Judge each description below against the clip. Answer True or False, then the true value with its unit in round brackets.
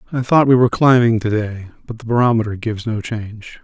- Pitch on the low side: True (115 Hz)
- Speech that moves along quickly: True (215 wpm)